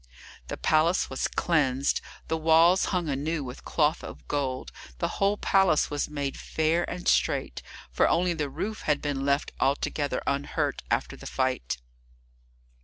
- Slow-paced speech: No, average, 150 wpm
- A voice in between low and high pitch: Yes, medium, 150 Hz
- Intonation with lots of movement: No, average, 3.4 semitones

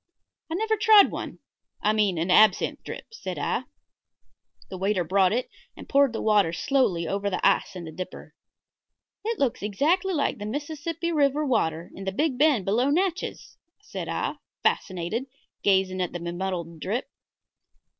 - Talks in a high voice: Yes, high, 215 Hz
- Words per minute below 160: No, average, 165 wpm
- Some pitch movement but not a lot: No, wide, 8.0 semitones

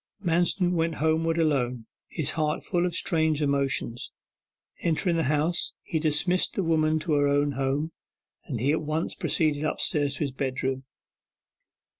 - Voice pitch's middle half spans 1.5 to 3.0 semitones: Yes, narrow, 2.6 semitones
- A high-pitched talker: No, medium, 155 Hz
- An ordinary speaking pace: Yes, average, 145 wpm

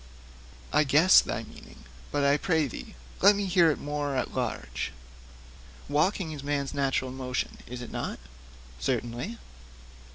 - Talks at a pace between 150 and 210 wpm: No, average, 140 wpm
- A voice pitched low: No, medium, 145 Hz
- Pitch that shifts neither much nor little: Yes, average, 3.5 semitones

